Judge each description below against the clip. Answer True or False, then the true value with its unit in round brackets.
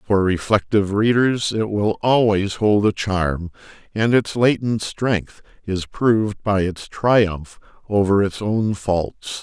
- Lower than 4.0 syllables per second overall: True (3.6 syllables/s)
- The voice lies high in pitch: False (100 Hz)